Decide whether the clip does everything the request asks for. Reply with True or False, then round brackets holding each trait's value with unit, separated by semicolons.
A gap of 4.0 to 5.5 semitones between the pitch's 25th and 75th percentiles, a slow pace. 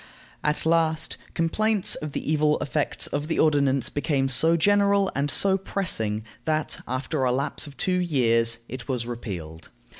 False (4.5 semitones; 155 wpm)